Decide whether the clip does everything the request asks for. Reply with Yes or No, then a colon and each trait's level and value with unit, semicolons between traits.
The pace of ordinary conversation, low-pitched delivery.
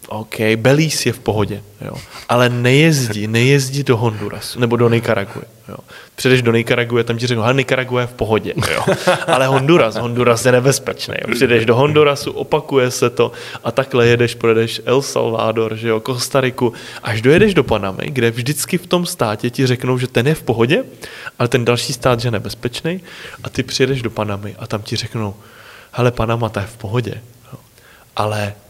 No: fast, 180 wpm; low, 120 Hz